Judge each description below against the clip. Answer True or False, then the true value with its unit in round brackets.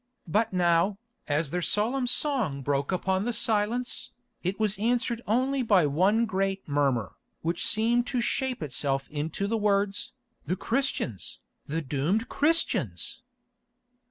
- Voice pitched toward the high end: True (200 Hz)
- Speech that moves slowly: True (130 wpm)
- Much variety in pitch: True (6.6 semitones)